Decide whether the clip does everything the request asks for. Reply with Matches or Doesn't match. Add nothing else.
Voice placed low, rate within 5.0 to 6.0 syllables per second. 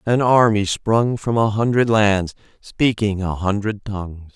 Doesn't match